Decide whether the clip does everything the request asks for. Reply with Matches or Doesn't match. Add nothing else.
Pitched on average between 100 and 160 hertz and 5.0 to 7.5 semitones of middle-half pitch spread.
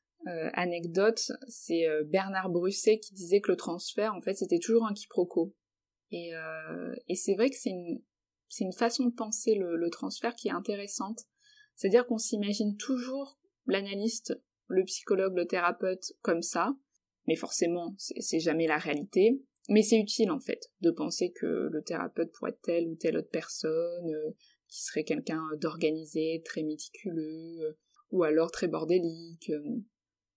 Doesn't match